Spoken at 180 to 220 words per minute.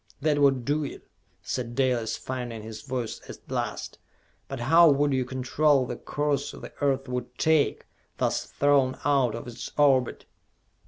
No: average, 155 wpm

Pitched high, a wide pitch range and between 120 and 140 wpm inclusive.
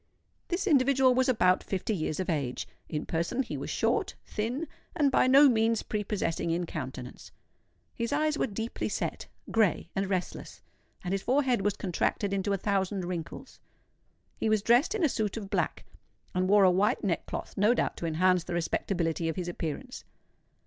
No: high, 200 Hz; wide, 5.8 semitones; average, 170 wpm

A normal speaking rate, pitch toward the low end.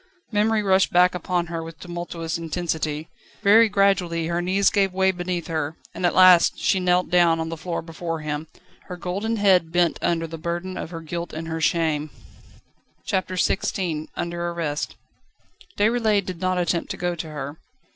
No: average, 170 wpm; medium, 175 Hz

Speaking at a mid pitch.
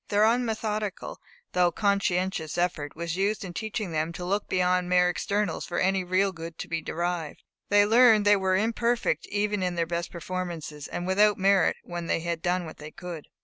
Yes: medium, 180 Hz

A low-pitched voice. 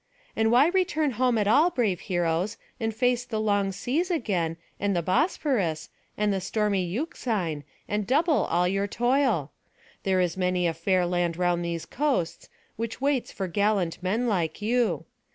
No: high, 205 Hz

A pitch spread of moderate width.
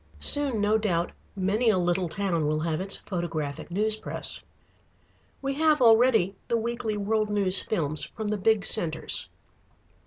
Yes: average, 4.2 semitones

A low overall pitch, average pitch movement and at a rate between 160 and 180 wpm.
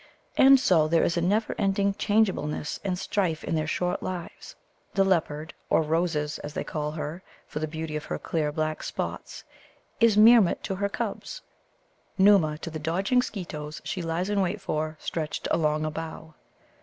No: medium, 165 Hz; average, 4.1 semitones; average, 175 wpm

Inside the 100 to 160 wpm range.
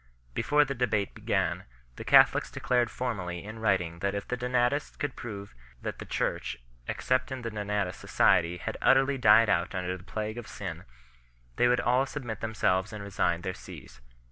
No: average, 180 wpm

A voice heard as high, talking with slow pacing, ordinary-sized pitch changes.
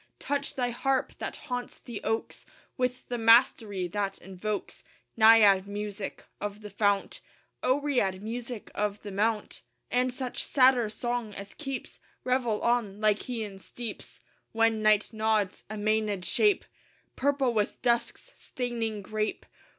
Yes: high, 220 Hz; slow, 130 wpm; average, 3.1 semitones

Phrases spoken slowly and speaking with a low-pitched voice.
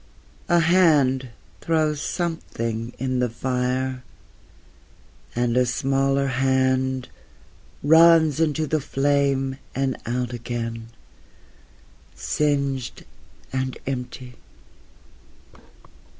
Yes: slow, 80 wpm; low, 130 Hz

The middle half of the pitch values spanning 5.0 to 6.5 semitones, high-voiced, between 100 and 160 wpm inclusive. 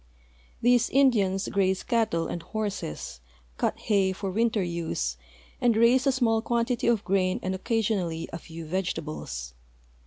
Yes: average, 5.3 semitones; high, 195 Hz; slow, 135 wpm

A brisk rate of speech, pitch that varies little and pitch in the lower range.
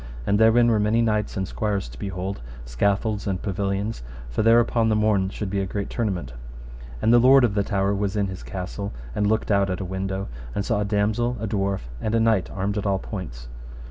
Yes: fast, 220 wpm; narrow, 2.1 semitones; low, 100 Hz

